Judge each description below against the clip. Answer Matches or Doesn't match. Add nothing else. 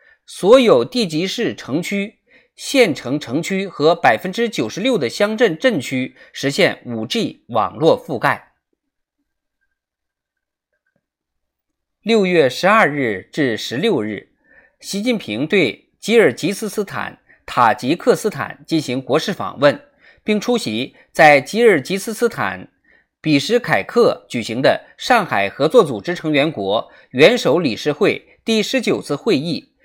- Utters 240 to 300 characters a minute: Doesn't match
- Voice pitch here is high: Matches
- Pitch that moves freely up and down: Matches